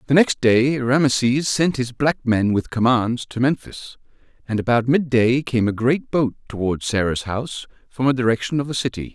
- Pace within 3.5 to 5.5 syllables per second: Yes, 5.0 syllables/s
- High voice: No, low, 125 Hz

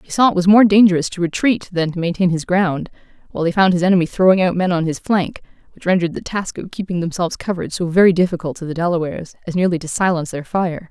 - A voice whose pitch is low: No, medium, 175 Hz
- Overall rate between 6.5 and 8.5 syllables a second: Yes, 6.9 syllables/s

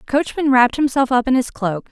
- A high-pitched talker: Yes, very high, 255 Hz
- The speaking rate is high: Yes, fast, 250 wpm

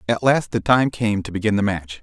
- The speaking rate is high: Yes, fast, 265 wpm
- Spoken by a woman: No, male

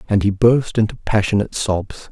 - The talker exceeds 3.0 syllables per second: Yes, 5.2 syllables/s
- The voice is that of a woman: No, male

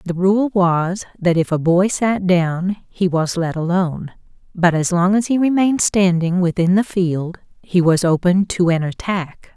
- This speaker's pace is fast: No, average, 180 wpm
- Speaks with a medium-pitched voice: Yes, medium, 180 Hz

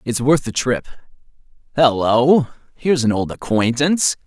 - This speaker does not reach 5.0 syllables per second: Yes, 4.4 syllables/s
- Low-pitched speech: Yes, low, 130 Hz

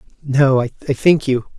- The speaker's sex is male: Yes, male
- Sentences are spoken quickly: No, average, 150 wpm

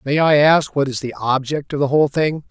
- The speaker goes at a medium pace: No, fast, 265 wpm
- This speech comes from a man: Yes, male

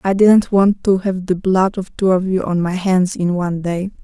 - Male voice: No, female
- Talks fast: Yes, fast, 255 wpm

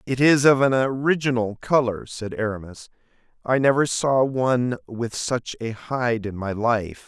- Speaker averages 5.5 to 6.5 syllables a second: No, 4.4 syllables/s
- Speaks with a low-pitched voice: Yes, low, 120 Hz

